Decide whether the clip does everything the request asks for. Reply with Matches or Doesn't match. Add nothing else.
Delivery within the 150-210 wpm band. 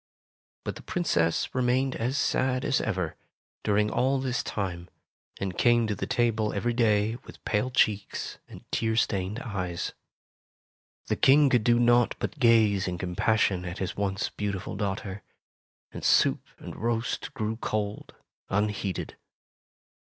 Doesn't match